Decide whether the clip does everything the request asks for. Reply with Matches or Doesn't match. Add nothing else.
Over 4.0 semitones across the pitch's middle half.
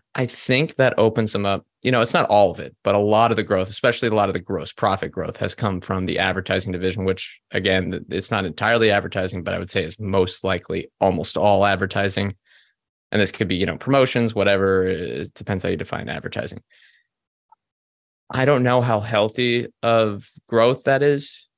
Doesn't match